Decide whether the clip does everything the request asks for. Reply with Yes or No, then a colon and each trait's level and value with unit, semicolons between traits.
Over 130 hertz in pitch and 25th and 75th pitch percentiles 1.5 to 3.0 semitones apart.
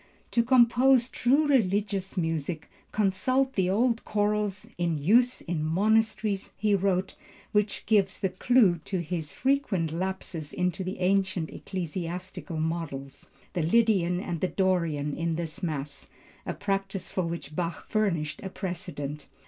No: medium, 185 Hz; average, 4.0 semitones